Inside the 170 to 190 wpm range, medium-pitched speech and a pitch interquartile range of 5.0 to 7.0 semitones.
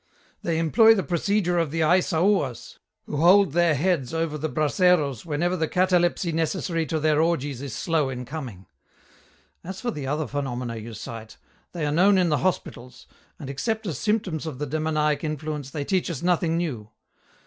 No: average, 175 wpm; medium, 160 Hz; average, 3.9 semitones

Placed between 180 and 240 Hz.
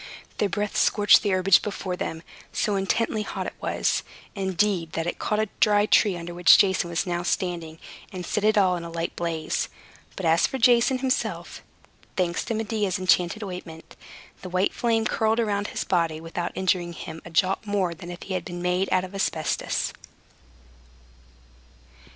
Yes: medium, 185 Hz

